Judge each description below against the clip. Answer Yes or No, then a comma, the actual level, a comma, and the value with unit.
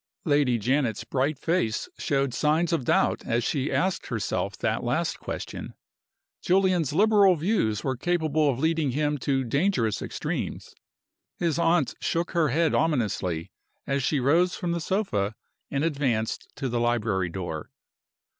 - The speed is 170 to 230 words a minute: No, average, 145 wpm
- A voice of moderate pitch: Yes, medium, 145 Hz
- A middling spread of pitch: No, wide, 5.8 semitones